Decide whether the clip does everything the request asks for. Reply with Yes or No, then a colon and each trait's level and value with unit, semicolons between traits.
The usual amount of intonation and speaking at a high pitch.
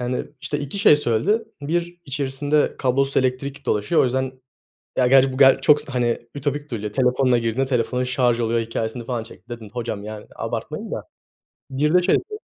No: average, 3.2 semitones; low, 130 Hz